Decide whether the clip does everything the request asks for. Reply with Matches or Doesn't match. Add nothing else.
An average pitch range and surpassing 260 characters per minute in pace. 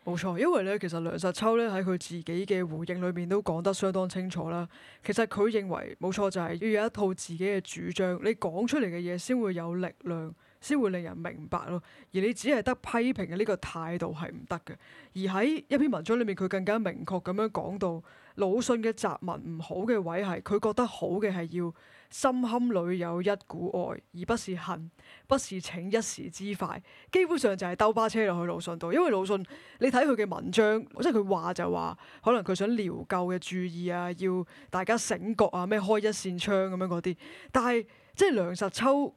Matches